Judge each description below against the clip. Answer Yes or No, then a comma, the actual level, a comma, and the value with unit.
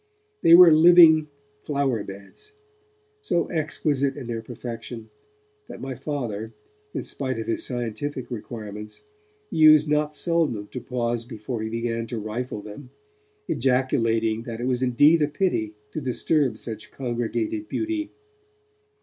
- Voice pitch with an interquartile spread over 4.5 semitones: Yes, average, 5.0 semitones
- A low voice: Yes, low, 125 Hz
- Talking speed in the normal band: No, slow, 130 wpm